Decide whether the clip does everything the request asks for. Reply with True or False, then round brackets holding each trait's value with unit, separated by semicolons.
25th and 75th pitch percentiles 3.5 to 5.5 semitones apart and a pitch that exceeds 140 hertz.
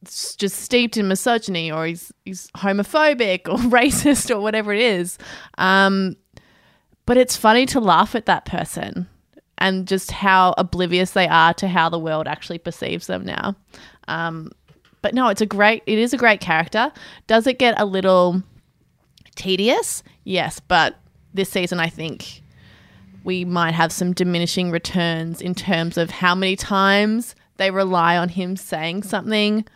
True (3.8 semitones; 190 Hz)